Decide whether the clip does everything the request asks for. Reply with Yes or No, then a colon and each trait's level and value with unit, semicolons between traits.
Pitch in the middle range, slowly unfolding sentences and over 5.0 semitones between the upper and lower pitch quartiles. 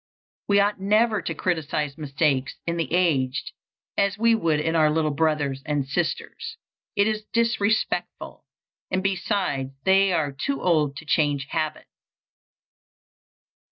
Yes: medium, 165 Hz; slow, 130 wpm; wide, 5.4 semitones